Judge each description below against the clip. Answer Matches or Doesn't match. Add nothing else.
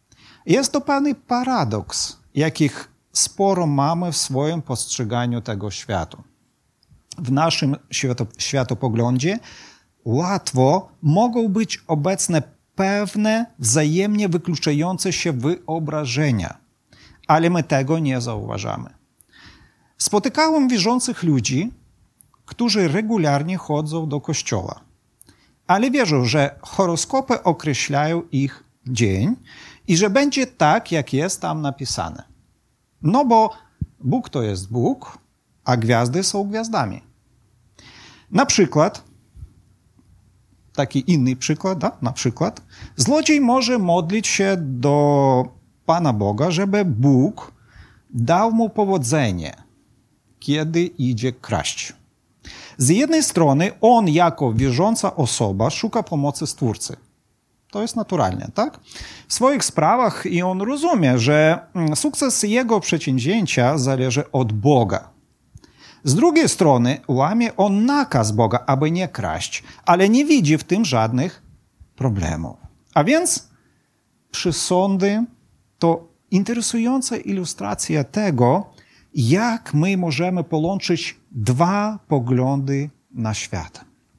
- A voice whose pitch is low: Doesn't match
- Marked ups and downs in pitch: Matches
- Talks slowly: Matches